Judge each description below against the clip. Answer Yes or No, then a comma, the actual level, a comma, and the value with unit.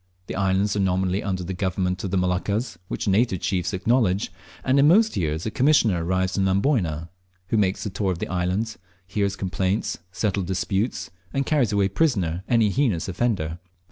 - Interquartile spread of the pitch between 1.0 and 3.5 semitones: Yes, average, 3.2 semitones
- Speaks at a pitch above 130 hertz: No, very low, 95 Hz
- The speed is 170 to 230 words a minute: Yes, average, 180 wpm